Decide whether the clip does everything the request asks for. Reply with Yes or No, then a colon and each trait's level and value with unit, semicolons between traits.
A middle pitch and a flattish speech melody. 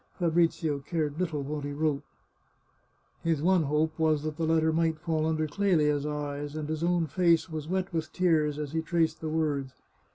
Yes: medium, 155 Hz; narrow, 1.9 semitones